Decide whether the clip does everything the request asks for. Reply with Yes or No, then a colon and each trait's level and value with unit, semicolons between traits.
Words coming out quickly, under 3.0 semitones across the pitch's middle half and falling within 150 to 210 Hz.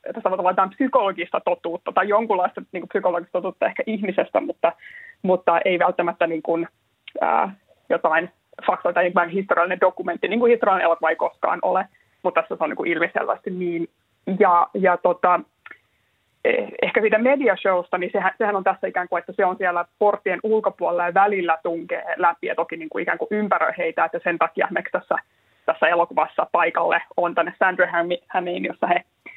Yes: fast, 175 wpm; narrow, 2.4 semitones; medium, 185 Hz